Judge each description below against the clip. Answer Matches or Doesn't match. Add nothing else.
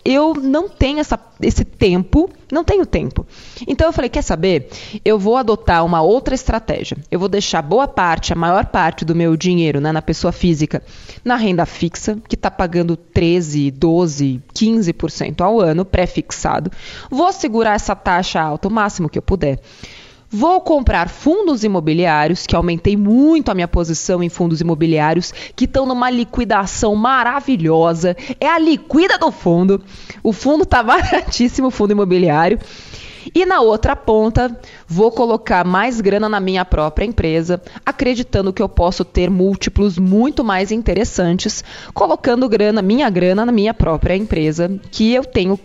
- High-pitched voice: Matches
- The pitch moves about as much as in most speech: Doesn't match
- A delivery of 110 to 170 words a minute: Matches